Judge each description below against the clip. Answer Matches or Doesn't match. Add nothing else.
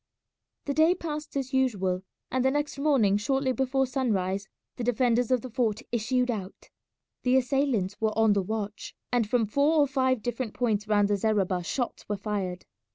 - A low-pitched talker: Doesn't match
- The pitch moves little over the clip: Doesn't match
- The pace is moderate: Matches